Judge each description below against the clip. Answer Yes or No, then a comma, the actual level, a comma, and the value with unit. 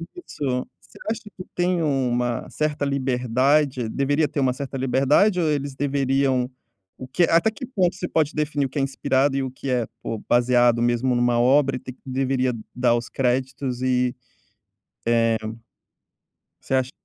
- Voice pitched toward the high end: No, low, 130 Hz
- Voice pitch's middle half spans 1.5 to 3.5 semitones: Yes, narrow, 2.4 semitones